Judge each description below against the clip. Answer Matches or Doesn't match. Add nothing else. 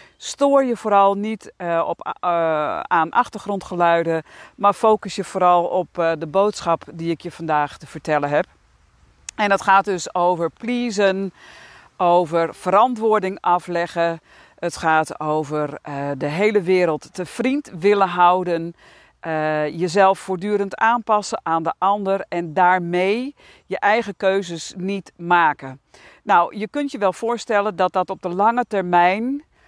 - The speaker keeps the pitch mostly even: Doesn't match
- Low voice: Doesn't match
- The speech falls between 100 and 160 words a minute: Matches